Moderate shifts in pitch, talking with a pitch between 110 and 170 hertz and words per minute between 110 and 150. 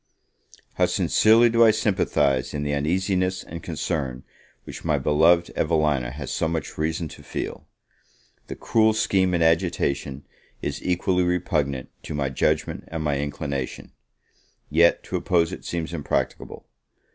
No: average, 3.9 semitones; very low, 80 Hz; average, 140 wpm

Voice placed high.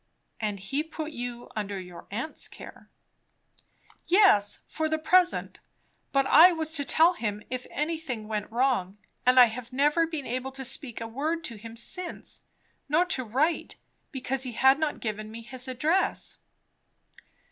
Yes: very high, 265 Hz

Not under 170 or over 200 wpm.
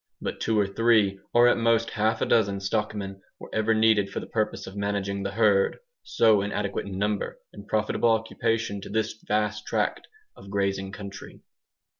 Yes: average, 175 wpm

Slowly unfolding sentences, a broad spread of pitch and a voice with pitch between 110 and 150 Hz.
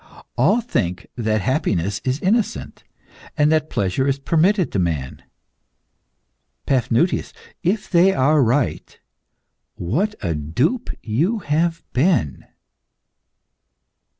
Yes: slow, 100 wpm; wide, 8.9 semitones; medium, 140 Hz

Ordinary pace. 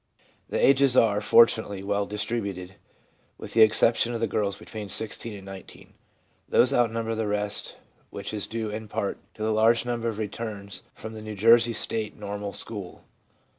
Yes: average, 170 wpm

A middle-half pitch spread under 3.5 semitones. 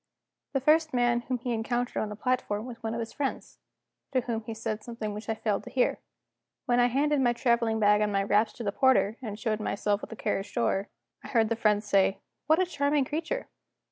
Yes: average, 3.0 semitones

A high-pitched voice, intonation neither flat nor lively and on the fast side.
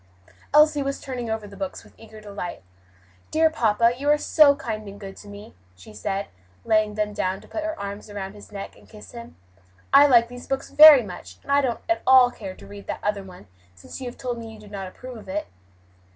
Yes: high, 215 Hz; average, 4.6 semitones; fast, 230 wpm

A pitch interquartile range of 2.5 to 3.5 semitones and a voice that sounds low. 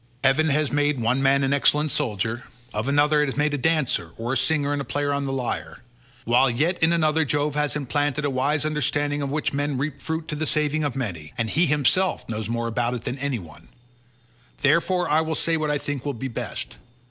No: average, 2.8 semitones; medium, 145 Hz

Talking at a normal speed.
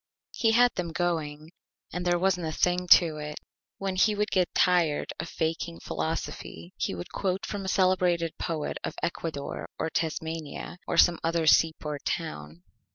Yes: average, 160 wpm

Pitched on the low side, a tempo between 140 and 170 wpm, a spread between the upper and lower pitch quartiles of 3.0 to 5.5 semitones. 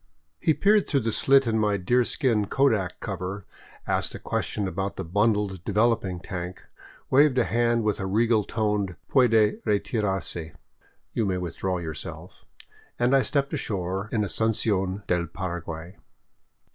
Yes: low, 105 Hz; average, 150 wpm; average, 3.9 semitones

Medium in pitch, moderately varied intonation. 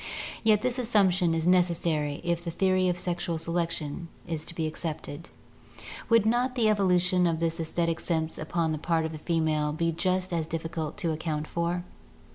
No: medium, 170 Hz; narrow, 2.3 semitones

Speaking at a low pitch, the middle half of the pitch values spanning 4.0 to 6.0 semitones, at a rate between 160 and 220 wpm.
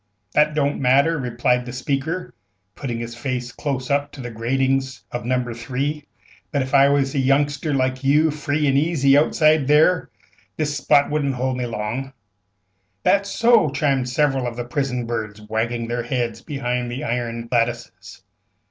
No: low, 130 Hz; average, 2.9 semitones; average, 165 wpm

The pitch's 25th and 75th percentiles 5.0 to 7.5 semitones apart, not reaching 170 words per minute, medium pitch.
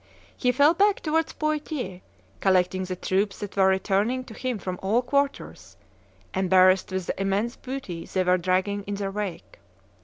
No: average, 5.3 semitones; average, 160 wpm; high, 200 Hz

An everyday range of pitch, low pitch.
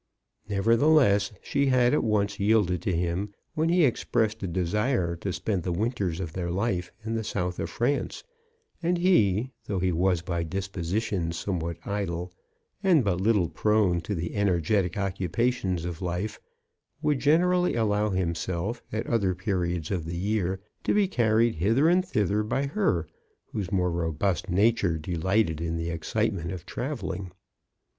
Yes: average, 4.4 semitones; low, 100 Hz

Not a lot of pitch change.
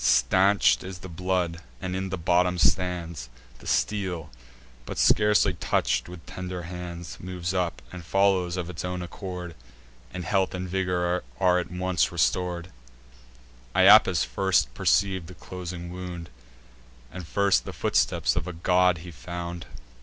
Yes: narrow, 1.1 semitones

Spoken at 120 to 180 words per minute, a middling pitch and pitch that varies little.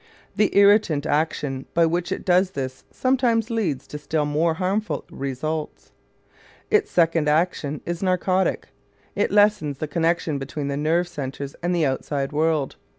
No: average, 145 wpm; medium, 160 Hz; average, 3.9 semitones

